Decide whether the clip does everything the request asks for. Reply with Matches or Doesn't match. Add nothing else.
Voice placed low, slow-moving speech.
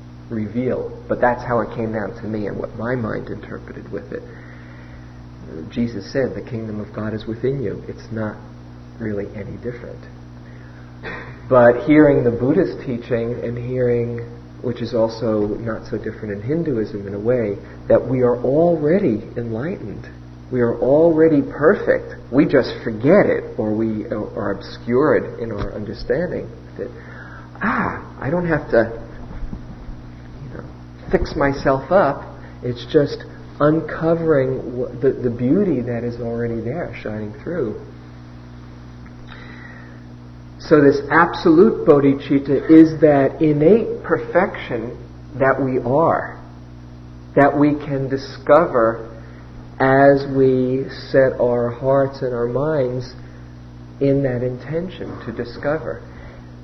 Matches